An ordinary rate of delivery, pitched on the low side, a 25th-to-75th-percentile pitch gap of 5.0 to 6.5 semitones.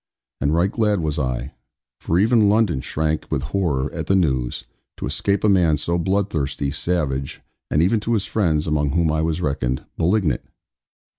Yes: average, 170 wpm; very low, 80 Hz; average, 5.3 semitones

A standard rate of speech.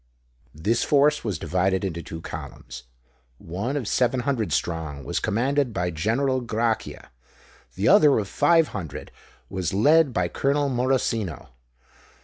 No: slow, 130 wpm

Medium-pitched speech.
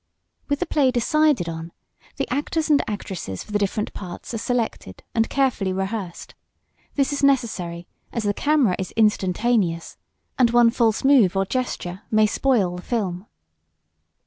No: high, 220 Hz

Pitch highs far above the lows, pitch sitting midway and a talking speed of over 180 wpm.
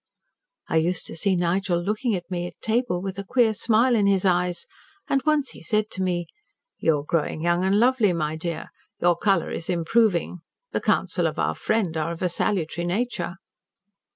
No: average, 3.8 semitones; medium, 180 Hz; average, 190 wpm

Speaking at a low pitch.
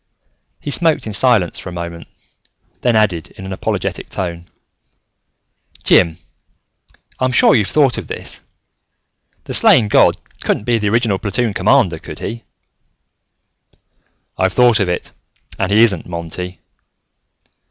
Yes: low, 100 Hz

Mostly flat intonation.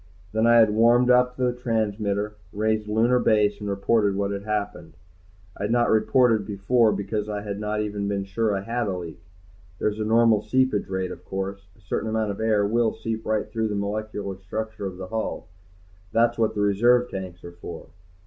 Yes: narrow, 2.1 semitones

